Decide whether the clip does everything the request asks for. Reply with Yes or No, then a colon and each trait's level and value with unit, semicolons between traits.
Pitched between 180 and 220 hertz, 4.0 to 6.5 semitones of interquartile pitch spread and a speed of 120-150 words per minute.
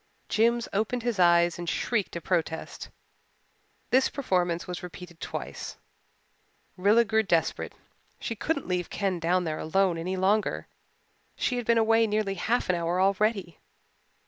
Yes: high, 190 Hz; average, 4.3 semitones; average, 145 wpm